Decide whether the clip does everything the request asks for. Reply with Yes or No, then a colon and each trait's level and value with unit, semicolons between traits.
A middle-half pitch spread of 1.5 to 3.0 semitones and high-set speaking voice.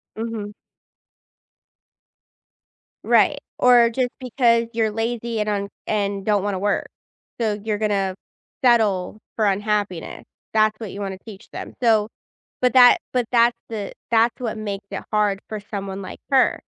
Yes: narrow, 2.4 semitones; high, 215 Hz